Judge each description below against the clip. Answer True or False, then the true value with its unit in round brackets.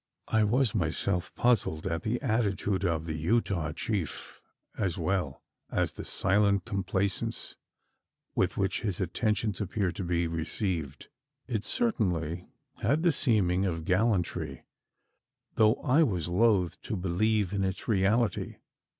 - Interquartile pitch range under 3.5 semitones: False (4.1 semitones)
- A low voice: True (95 Hz)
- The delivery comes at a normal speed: False (130 wpm)